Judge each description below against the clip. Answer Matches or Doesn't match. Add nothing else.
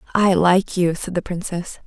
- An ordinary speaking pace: Matches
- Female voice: Matches